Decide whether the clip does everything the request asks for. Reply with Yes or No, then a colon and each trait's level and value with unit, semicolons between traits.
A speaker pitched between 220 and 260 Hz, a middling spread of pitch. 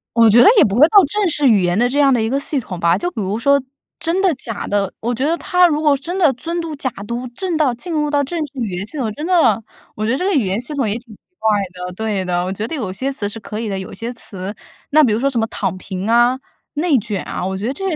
No: high, 245 Hz; wide, 6.2 semitones